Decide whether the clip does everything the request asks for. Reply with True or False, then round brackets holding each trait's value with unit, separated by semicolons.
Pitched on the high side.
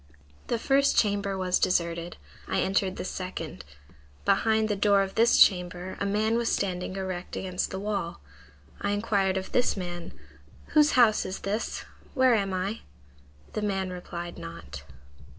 True (195 Hz)